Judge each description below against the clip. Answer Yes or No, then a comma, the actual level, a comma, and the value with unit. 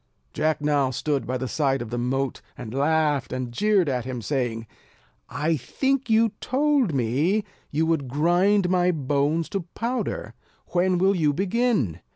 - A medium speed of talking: Yes, average, 160 wpm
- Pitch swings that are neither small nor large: No, wide, 6.2 semitones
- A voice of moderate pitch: Yes, medium, 150 Hz